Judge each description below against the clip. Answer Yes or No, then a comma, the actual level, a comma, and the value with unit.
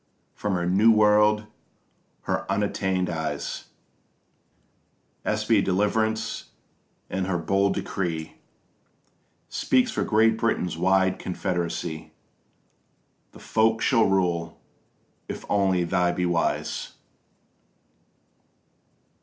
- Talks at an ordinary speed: No, slow, 85 wpm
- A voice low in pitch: Yes, very low, 95 Hz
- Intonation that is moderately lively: Yes, average, 3.3 semitones